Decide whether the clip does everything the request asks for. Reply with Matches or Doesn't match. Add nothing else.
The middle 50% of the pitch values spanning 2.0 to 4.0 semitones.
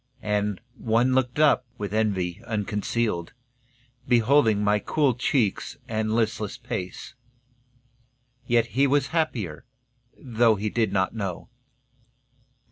Matches